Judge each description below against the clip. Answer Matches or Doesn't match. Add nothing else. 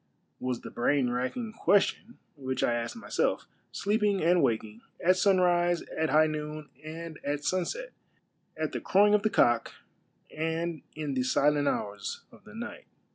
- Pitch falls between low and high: Matches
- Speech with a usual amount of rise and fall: Doesn't match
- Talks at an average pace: Matches